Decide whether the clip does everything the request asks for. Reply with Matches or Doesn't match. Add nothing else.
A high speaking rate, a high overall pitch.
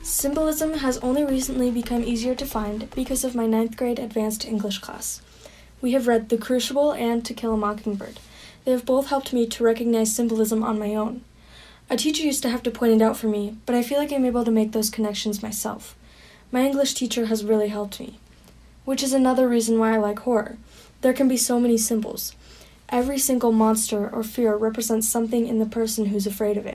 Matches